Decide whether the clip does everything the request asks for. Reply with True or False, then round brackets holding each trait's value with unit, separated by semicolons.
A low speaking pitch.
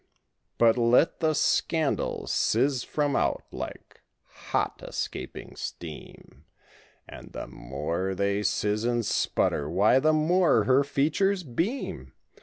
True (125 Hz)